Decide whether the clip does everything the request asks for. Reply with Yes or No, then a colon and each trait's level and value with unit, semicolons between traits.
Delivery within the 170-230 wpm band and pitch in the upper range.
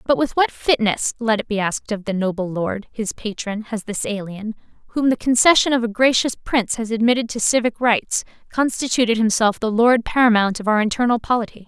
Yes: average, 195 wpm; high, 225 Hz